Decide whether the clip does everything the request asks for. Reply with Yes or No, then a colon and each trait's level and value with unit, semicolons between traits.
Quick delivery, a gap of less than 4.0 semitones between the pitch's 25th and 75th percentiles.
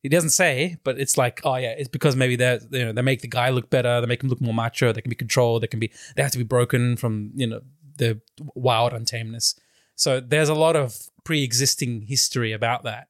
Yes: fast, 245 wpm; narrow, 2.6 semitones